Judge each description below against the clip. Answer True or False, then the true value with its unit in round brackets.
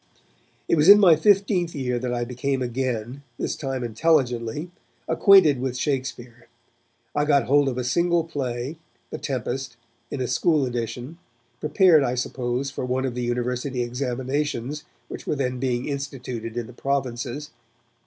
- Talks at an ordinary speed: True (155 wpm)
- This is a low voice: True (130 Hz)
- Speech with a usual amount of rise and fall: True (3.3 semitones)